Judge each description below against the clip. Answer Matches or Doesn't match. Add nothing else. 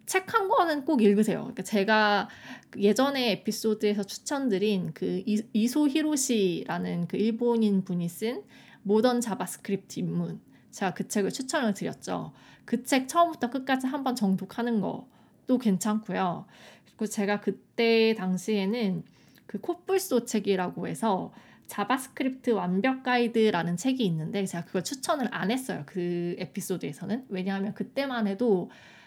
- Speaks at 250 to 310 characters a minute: Matches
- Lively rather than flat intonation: Doesn't match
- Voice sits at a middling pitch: Doesn't match